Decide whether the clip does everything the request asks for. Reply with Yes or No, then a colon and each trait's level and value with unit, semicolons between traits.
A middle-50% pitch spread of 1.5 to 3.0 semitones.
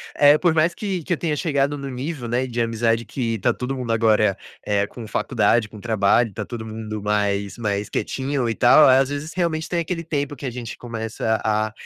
No: average, 4.7 semitones